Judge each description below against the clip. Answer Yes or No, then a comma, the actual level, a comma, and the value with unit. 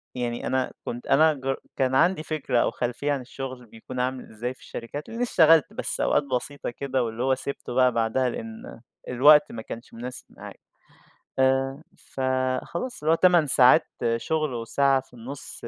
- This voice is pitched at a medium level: No, low, 130 Hz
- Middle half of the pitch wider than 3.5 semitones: No, average, 3.2 semitones